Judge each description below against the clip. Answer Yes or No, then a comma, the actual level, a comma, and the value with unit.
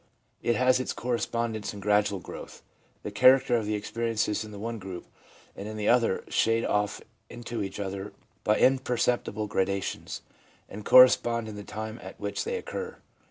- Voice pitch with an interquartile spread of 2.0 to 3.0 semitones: Yes, narrow, 2.6 semitones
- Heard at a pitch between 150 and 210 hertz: No, low, 110 Hz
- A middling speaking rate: Yes, average, 165 wpm